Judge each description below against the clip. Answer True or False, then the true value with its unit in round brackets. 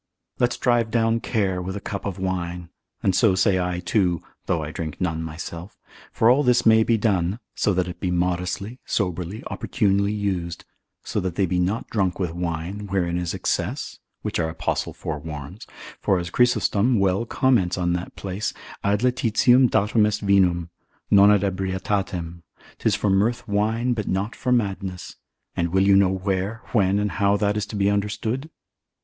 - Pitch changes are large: False (3.1 semitones)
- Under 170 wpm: False (175 wpm)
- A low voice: True (100 Hz)